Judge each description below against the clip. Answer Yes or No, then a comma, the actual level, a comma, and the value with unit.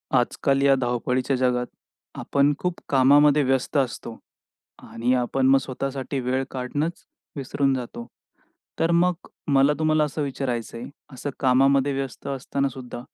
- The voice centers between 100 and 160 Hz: Yes, low, 135 Hz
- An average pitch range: No, narrow, 2.0 semitones